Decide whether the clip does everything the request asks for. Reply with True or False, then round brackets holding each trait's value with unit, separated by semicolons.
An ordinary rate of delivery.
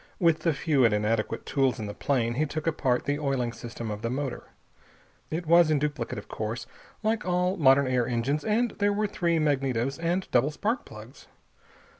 True (190 wpm)